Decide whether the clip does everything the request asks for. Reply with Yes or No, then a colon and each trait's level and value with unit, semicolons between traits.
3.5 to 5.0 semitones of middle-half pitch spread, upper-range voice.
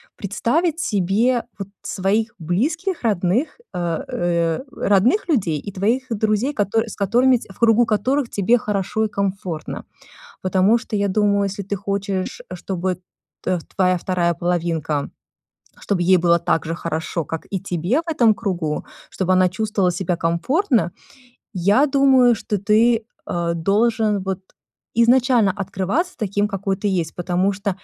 Yes: average, 4.2 semitones; high, 200 Hz